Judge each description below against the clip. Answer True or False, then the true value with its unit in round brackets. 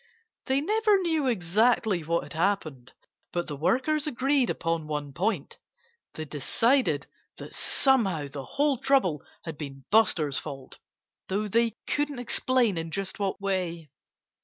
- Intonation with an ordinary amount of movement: False (8.6 semitones)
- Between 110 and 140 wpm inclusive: True (135 wpm)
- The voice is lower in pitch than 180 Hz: False (195 Hz)